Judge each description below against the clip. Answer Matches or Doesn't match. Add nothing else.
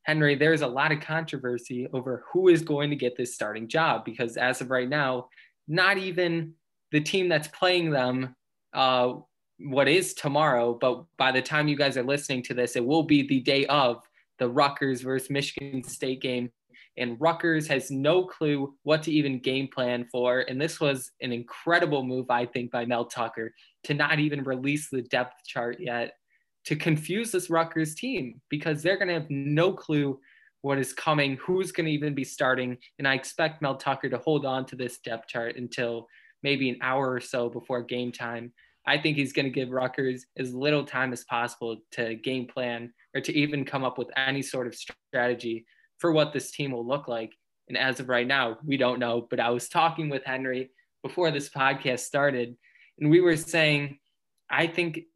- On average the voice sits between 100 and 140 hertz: Matches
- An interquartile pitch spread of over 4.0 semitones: Doesn't match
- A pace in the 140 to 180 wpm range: Doesn't match